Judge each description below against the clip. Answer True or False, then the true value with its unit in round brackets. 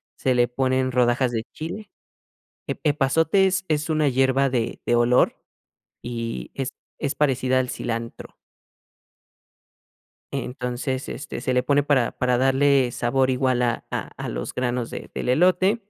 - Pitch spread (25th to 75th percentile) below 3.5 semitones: True (2.7 semitones)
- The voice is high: False (130 Hz)